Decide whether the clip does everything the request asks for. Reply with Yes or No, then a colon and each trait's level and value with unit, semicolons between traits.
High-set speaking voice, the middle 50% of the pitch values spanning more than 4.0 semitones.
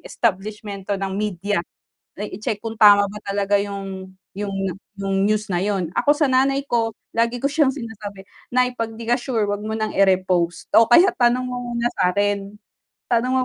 No: high, 210 Hz; average, 3.3 semitones